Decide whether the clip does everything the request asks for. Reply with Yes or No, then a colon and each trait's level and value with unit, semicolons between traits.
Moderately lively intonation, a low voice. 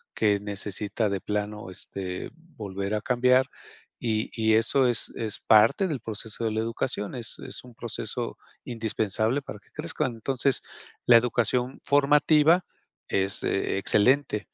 Yes: average, 3.7 semitones; low, 115 Hz